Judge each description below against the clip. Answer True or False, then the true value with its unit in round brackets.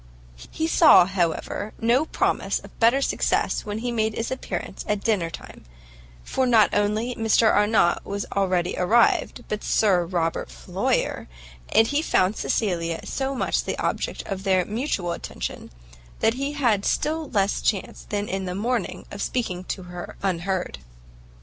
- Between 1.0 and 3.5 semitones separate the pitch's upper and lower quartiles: False (4.3 semitones)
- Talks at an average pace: True (155 wpm)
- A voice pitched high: True (205 Hz)